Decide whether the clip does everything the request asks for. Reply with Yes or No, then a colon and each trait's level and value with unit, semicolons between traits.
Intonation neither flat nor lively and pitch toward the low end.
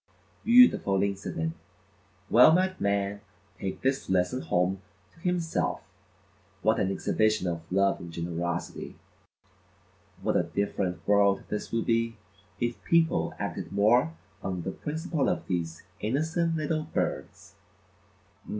No: wide, 8.5 semitones; low, 100 Hz